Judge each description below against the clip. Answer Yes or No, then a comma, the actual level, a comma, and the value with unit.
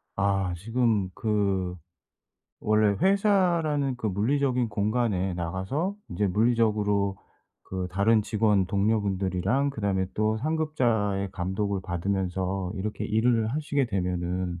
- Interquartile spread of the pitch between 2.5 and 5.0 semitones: Yes, average, 4.1 semitones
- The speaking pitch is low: Yes, low, 105 Hz